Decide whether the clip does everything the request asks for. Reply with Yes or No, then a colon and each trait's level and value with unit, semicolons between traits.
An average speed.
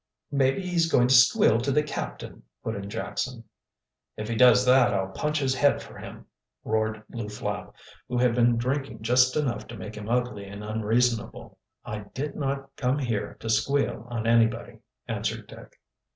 Yes: average, 175 wpm